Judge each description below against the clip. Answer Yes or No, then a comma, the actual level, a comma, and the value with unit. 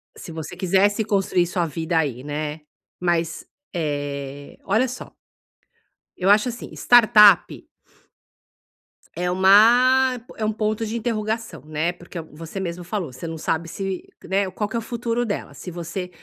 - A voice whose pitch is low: No, medium, 185 Hz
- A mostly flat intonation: No, average, 4.8 semitones